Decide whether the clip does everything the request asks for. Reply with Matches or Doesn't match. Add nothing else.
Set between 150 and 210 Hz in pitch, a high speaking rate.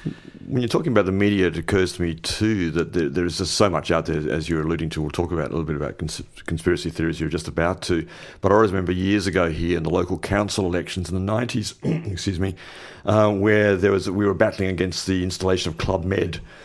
Doesn't match